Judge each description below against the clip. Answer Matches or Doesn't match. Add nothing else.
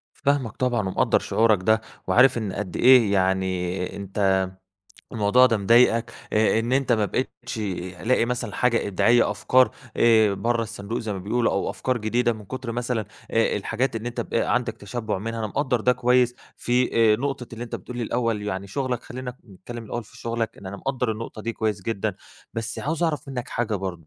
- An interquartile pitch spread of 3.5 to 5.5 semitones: Doesn't match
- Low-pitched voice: Matches